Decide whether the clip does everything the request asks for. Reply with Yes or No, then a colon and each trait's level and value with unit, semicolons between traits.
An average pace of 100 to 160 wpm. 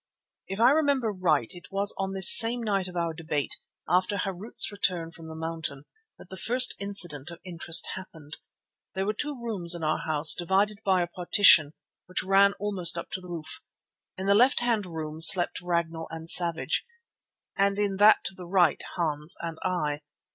No: average, 185 wpm